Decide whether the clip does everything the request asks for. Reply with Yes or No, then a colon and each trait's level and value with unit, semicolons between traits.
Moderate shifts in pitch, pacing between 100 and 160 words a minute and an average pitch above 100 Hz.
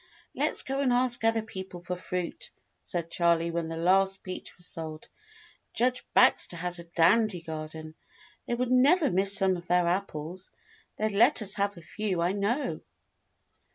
No: average, 4.7 semitones; average, 175 wpm; medium, 185 Hz